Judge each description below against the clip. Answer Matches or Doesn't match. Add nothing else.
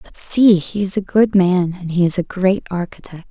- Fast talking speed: Matches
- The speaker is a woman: Matches